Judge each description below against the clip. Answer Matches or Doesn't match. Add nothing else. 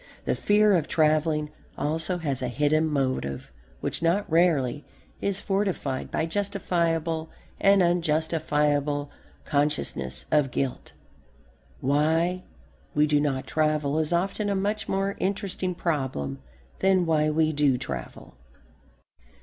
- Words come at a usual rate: Doesn't match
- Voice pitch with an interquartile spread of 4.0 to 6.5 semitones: Doesn't match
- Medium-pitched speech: Matches